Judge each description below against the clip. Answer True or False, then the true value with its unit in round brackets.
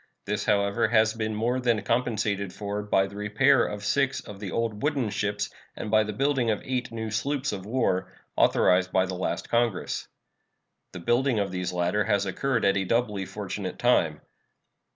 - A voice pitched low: True (105 Hz)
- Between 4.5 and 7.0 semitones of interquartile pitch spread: False (3.0 semitones)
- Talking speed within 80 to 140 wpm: False (180 wpm)